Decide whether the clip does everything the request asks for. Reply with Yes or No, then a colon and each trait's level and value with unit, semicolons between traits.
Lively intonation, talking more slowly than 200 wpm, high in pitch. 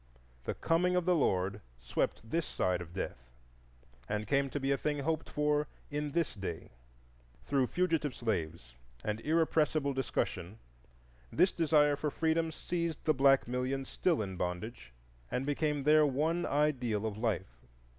No: wide, 6.4 semitones; average, 155 wpm; medium, 140 Hz